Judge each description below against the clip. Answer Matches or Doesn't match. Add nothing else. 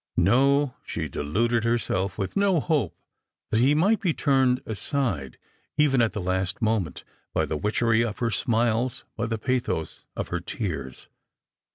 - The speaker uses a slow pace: Doesn't match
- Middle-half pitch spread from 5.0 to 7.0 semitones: Matches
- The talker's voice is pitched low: Matches